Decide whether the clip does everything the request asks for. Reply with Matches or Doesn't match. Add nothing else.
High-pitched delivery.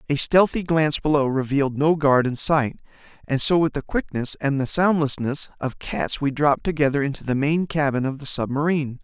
Doesn't match